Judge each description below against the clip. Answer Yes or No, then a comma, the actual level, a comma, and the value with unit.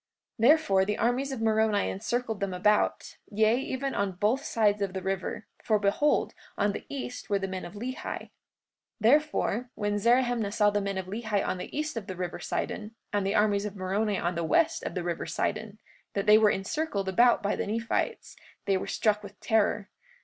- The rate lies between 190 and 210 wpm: Yes, average, 200 wpm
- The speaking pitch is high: Yes, high, 210 Hz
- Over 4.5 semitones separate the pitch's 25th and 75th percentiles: No, average, 2.8 semitones